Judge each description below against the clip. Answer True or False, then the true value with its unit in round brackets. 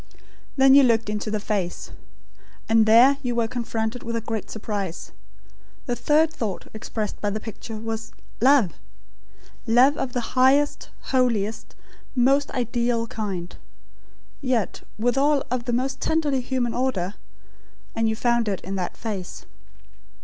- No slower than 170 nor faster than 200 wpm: False (140 wpm)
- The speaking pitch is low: False (235 Hz)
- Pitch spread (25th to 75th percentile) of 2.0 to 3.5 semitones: True (3.0 semitones)